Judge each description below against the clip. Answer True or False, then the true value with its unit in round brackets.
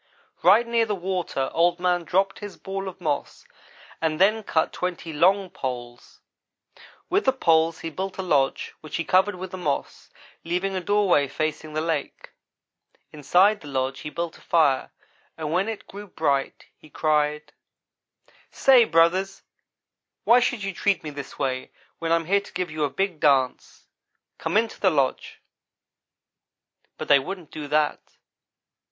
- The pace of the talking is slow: False (160 wpm)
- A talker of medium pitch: True (170 Hz)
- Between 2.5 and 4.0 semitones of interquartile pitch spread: False (4.4 semitones)